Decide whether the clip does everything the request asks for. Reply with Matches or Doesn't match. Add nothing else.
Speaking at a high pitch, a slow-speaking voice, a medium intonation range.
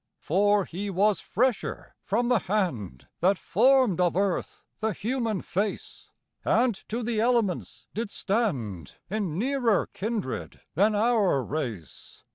Matches